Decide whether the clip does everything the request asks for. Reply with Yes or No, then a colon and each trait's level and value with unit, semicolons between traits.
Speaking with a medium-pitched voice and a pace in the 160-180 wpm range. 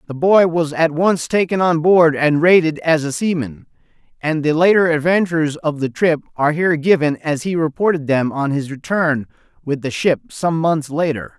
No: medium, 160 Hz; average, 190 wpm